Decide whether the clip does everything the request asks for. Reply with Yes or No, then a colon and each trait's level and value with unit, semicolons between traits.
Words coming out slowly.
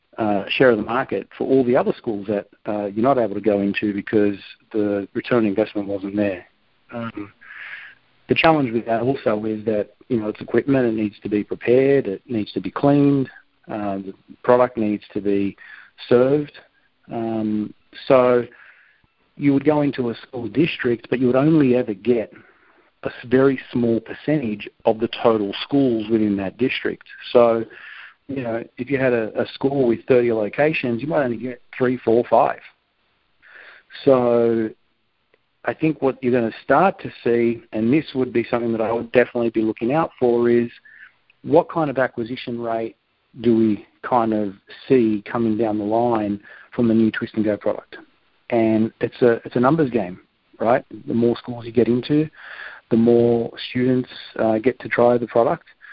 No: average, 180 wpm